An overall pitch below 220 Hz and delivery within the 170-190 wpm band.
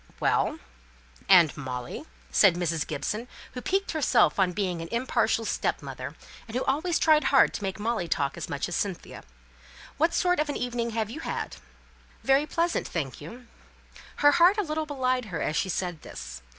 No: high, 230 Hz; average, 175 wpm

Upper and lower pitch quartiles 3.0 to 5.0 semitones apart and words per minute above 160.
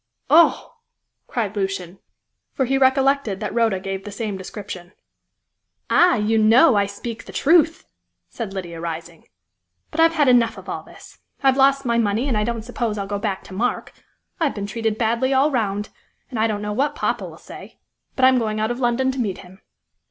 Yes: average, 4.6 semitones; average, 195 wpm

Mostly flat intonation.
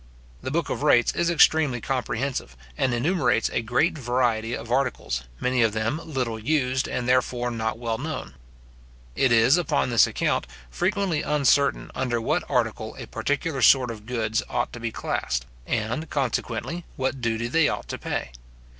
No: average, 3.7 semitones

